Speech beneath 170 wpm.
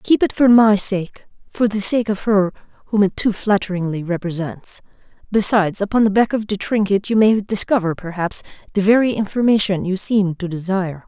No: average, 175 wpm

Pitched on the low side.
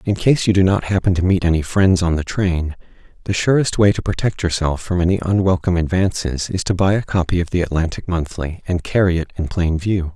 Yes: very low, 90 Hz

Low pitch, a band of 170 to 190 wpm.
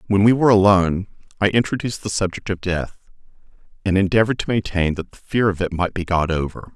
No: low, 100 Hz; fast, 205 wpm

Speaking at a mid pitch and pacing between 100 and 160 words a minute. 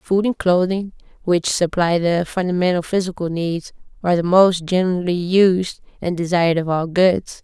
Yes: medium, 180 Hz; average, 155 wpm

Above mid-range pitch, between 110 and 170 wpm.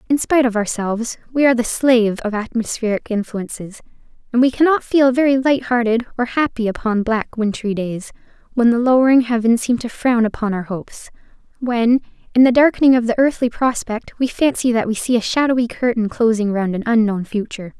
No: high, 235 Hz; average, 180 wpm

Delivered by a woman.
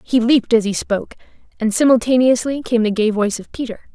Yes: female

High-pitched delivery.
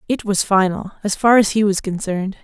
Yes: high, 200 Hz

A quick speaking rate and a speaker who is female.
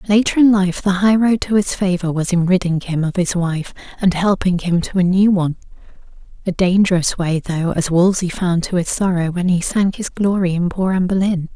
Yes: fast, 215 wpm; female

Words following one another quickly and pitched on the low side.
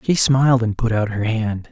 Yes: fast, 245 wpm; low, 115 Hz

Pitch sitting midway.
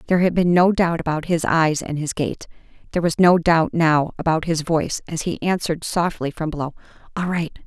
Yes: medium, 165 Hz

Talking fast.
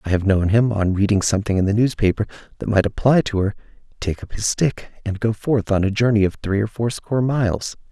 Yes: fast, 225 wpm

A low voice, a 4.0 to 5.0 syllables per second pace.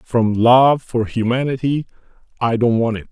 Yes: low, 120 Hz; 4.6 syllables/s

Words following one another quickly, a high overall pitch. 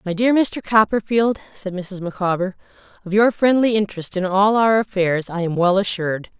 No: average, 180 wpm; high, 200 Hz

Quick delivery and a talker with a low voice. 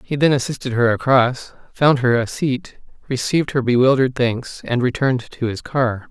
No: average, 175 wpm; low, 130 Hz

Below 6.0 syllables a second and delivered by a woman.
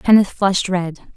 Yes: 4.9 syllables/s; female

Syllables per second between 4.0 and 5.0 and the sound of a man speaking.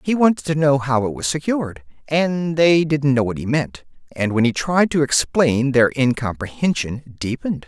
Yes: 4.8 syllables/s; male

